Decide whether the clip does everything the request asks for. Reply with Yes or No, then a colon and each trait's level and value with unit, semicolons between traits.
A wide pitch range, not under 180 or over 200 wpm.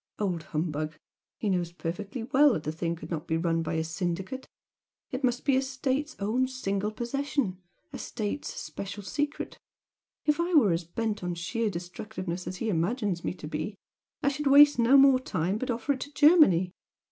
Yes: wide, 7.2 semitones; average, 185 wpm